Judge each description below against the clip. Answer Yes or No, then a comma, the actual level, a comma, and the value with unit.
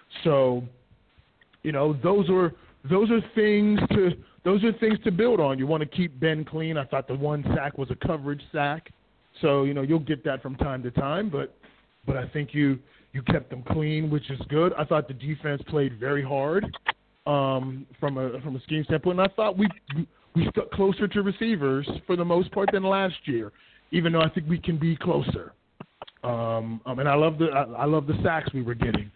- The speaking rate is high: Yes, fast, 215 wpm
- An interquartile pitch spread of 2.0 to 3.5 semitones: No, average, 4.5 semitones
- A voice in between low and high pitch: Yes, medium, 150 Hz